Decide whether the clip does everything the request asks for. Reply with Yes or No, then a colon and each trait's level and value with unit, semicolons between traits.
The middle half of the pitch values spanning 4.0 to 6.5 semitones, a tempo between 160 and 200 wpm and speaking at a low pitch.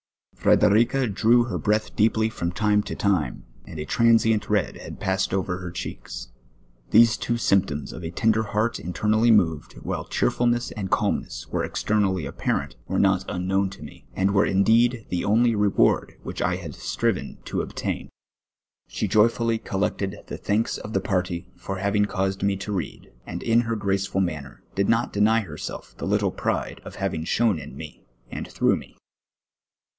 No: average, 3.4 semitones; average, 175 wpm; low, 100 Hz